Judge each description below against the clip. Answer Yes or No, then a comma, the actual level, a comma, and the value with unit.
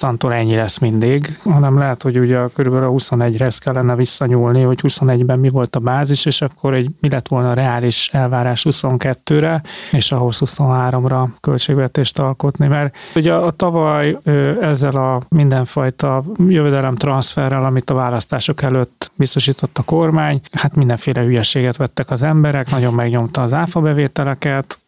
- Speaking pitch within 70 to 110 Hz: No, low, 135 Hz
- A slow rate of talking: No, average, 150 wpm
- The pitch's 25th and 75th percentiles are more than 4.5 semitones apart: No, narrow, 2.5 semitones